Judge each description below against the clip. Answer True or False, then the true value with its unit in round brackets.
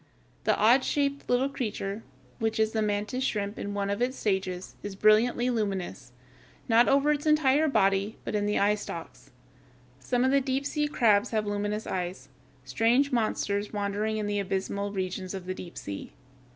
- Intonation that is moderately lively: True (3.8 semitones)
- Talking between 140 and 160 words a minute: False (170 wpm)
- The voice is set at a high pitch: True (210 Hz)